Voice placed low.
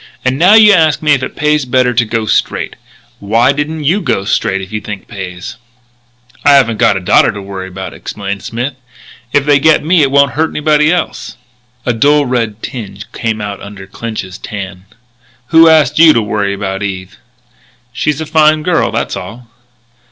Yes: low, 120 Hz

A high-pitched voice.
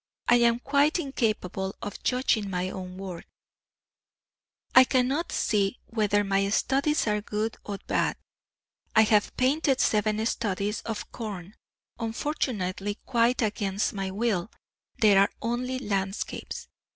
Yes: high, 215 Hz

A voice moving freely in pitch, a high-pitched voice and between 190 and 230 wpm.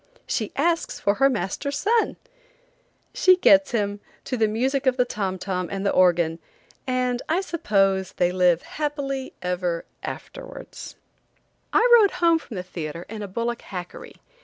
No: wide, 7.3 semitones; high, 220 Hz; average, 155 wpm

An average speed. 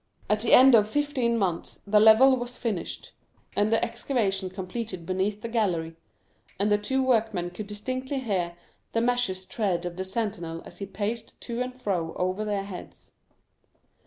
Yes: average, 165 wpm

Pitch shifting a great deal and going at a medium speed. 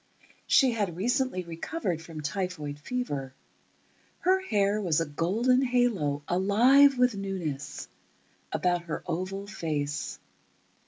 No: wide, 7.1 semitones; slow, 110 wpm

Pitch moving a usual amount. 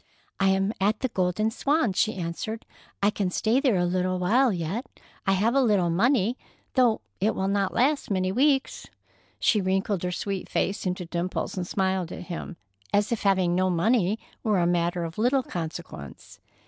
Yes: average, 3.6 semitones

